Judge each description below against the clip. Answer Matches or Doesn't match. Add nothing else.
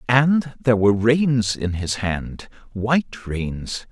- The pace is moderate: Doesn't match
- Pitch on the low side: Matches